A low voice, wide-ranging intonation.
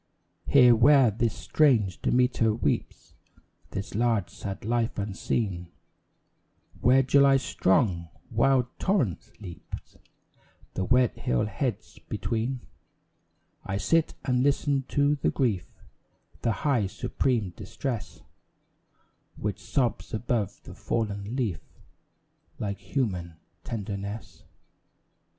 No: low, 115 Hz; average, 4.7 semitones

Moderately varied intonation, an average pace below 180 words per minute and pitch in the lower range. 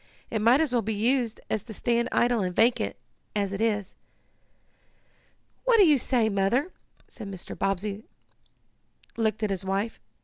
No: average, 3.4 semitones; average, 160 wpm; high, 220 Hz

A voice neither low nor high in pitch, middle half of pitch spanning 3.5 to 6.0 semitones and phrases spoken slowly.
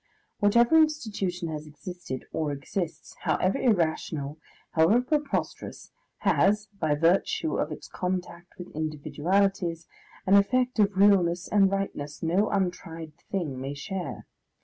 Yes: medium, 180 Hz; average, 4.2 semitones; slow, 120 wpm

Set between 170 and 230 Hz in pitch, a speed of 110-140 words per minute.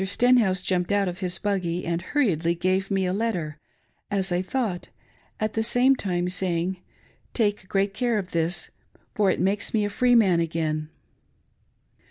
No: high, 190 Hz; average, 175 wpm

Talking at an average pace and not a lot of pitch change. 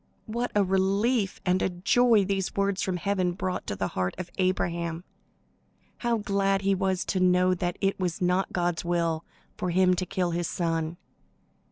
Yes: average, 175 wpm; narrow, 2.0 semitones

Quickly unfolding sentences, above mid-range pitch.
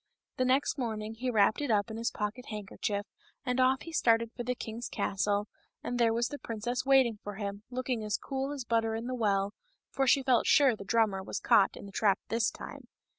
Yes: fast, 220 wpm; high, 230 Hz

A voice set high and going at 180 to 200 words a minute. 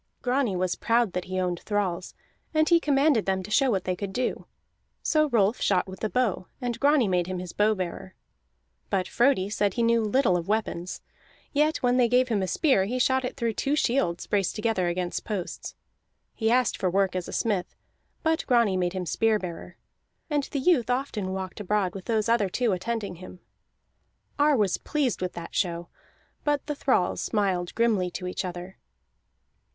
Yes: high, 210 Hz; average, 190 wpm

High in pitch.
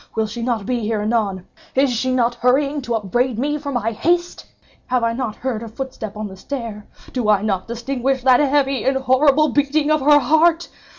Yes: very high, 250 Hz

